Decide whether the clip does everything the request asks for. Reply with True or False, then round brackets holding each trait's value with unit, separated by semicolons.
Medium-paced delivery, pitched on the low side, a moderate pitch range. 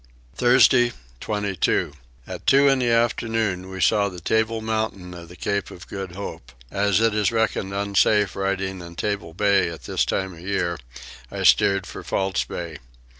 True (170 wpm; 100 Hz; 3.3 semitones)